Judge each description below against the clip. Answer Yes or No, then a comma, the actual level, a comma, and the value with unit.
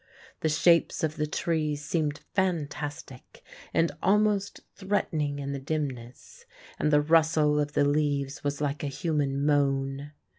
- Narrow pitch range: Yes, narrow, 2.2 semitones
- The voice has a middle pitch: Yes, medium, 150 Hz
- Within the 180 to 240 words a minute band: No, average, 140 wpm